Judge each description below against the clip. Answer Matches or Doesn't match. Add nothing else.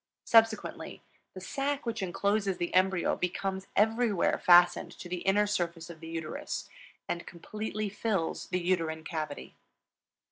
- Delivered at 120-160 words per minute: Matches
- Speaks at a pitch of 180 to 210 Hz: Matches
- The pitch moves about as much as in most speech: Matches